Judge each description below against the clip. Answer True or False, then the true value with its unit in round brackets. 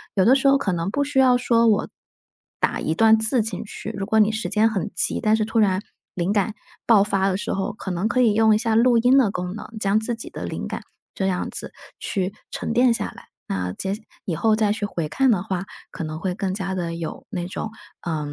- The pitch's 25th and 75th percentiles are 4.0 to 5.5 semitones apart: False (3.2 semitones)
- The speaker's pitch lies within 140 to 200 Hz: False (210 Hz)